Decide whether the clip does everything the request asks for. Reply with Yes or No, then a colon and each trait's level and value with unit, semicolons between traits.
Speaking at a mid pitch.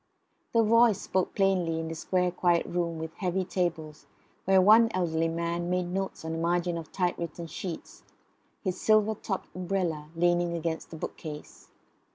Yes: medium, 175 Hz